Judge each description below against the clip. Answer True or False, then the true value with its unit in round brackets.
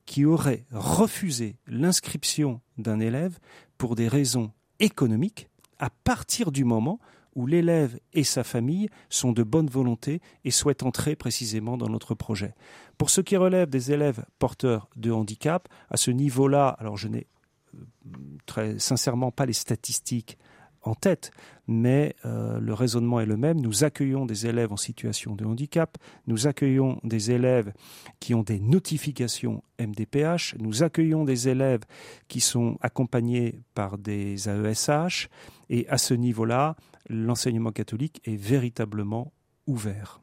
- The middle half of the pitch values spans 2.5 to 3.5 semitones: False (4.3 semitones)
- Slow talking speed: True (140 wpm)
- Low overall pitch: True (125 Hz)